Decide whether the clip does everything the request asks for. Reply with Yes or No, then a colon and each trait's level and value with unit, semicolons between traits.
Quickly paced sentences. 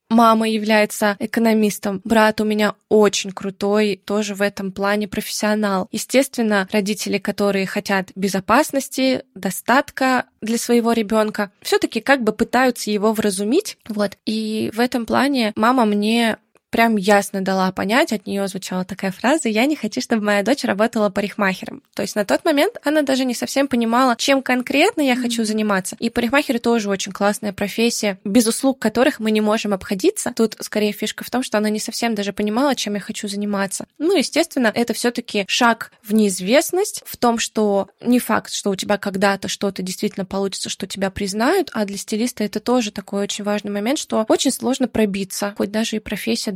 Yes: fast, 175 wpm